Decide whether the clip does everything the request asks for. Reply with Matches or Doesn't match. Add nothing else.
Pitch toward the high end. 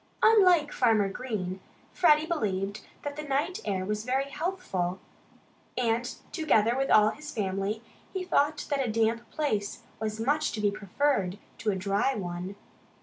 Matches